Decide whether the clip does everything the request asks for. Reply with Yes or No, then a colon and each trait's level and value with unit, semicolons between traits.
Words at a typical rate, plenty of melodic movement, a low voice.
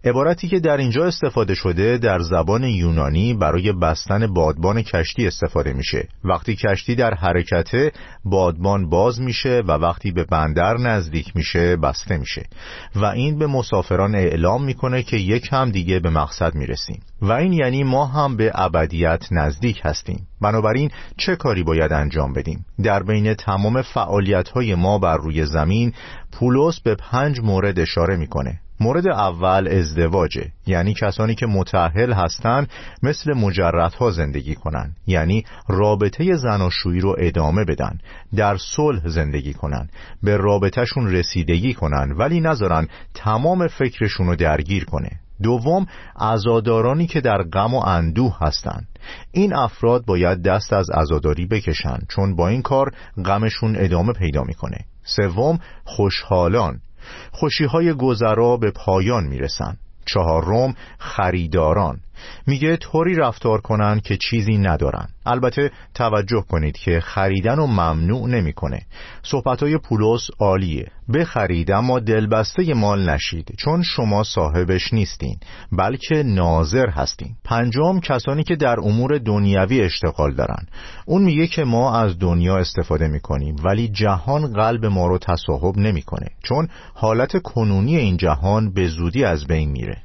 Yes: average, 135 wpm; wide, 5.8 semitones; low, 100 Hz